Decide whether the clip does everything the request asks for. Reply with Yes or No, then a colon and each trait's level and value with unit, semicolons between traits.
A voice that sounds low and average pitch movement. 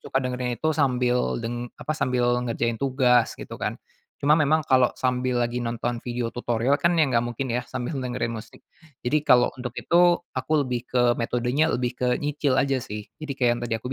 No: low, 125 Hz; narrow, 1.9 semitones